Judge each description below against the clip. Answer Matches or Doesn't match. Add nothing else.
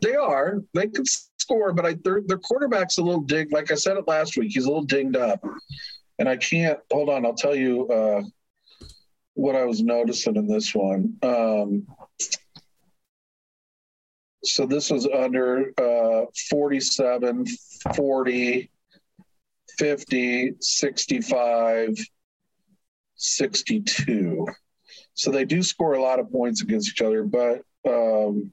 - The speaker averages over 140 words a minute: Doesn't match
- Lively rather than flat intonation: Matches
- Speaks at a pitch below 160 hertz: Matches